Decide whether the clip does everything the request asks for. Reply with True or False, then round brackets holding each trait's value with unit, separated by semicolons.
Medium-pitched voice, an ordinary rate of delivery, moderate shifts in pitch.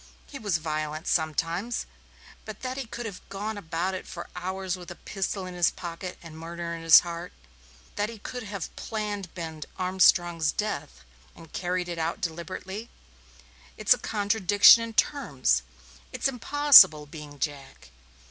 True (180 Hz; 150 wpm; 4.1 semitones)